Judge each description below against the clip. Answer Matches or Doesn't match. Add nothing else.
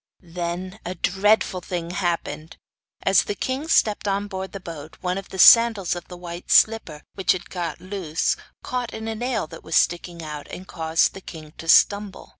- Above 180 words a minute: Matches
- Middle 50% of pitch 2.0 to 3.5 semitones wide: Matches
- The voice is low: Doesn't match